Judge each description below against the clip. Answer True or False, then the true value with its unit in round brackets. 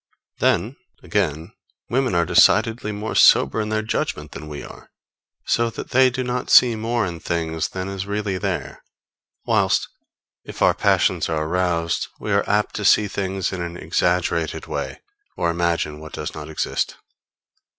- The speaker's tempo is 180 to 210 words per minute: False (160 wpm)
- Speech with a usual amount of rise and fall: True (4.4 semitones)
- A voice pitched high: False (95 Hz)